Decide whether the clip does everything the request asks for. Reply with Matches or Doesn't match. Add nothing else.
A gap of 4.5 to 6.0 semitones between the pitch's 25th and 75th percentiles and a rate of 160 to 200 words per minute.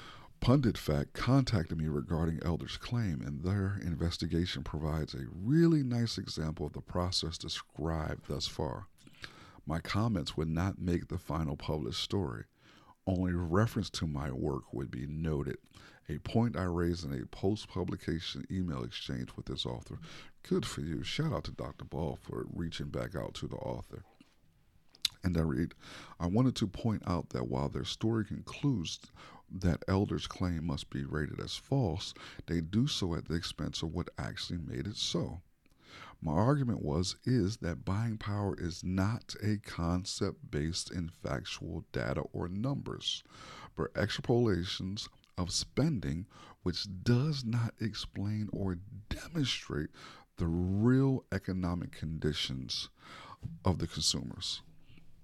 Doesn't match